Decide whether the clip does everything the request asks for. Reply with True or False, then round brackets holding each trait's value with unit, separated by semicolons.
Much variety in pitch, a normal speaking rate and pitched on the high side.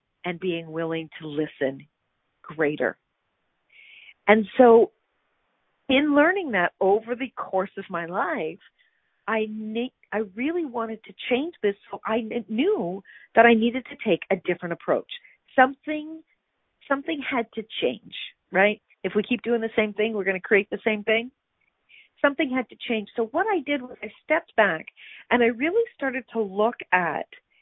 True (5.9 semitones; 165 wpm; 230 Hz)